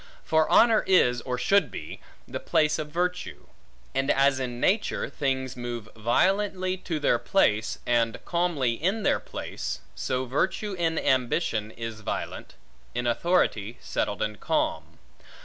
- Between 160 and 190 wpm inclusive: No, average, 140 wpm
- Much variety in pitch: Yes, wide, 7.1 semitones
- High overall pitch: No, low, 135 Hz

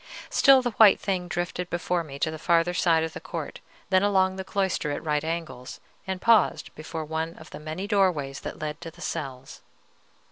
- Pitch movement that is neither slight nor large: Yes, average, 3.2 semitones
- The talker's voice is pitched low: No, medium, 170 Hz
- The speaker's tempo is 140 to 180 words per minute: No, average, 200 wpm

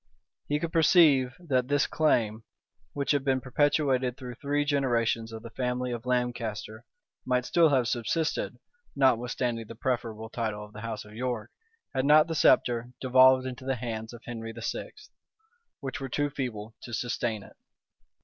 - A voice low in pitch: Yes, low, 125 Hz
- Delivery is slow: No, average, 160 wpm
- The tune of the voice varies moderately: Yes, average, 3.1 semitones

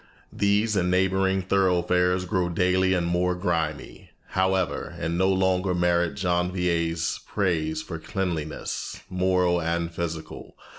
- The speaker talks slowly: Yes, slow, 110 wpm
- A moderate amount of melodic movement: No, narrow, 1.7 semitones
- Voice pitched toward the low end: Yes, very low, 90 Hz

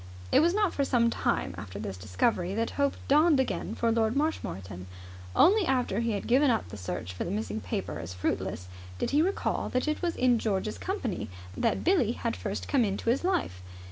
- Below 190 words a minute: No, fast, 205 wpm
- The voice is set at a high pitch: Yes, high, 230 Hz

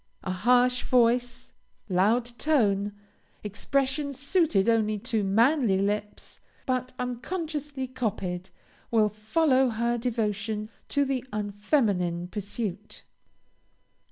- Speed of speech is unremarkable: No, slow, 95 wpm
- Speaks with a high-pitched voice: Yes, high, 230 Hz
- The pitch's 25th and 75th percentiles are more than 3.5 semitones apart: Yes, average, 3.9 semitones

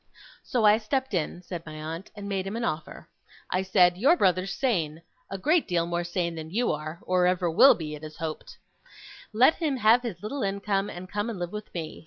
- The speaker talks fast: Yes, fast, 230 wpm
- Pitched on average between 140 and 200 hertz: Yes, medium, 185 Hz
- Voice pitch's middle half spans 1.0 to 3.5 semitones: No, average, 4.2 semitones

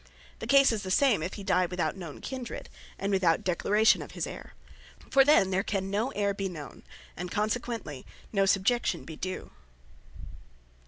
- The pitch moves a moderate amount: Yes, average, 3.4 semitones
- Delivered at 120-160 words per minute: No, average, 170 wpm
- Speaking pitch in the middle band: No, high, 195 Hz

